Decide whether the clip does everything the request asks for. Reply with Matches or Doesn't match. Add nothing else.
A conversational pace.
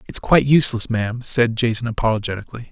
Matches